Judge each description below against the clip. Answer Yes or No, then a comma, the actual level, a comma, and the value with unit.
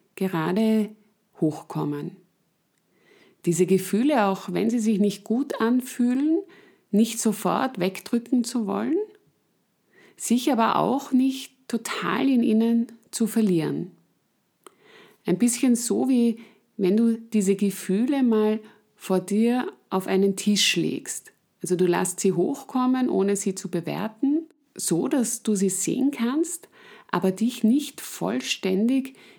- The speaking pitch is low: No, high, 220 Hz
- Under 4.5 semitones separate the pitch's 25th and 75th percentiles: No, average, 4.9 semitones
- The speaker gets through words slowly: Yes, slow, 120 wpm